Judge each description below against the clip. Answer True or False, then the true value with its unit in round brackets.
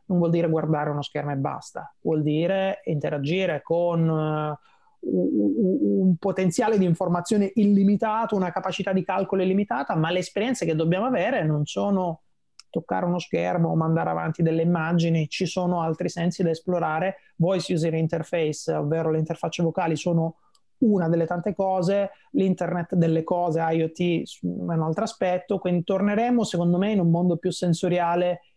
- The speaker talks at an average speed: True (160 wpm)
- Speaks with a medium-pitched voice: True (175 Hz)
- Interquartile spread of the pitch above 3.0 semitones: False (2.7 semitones)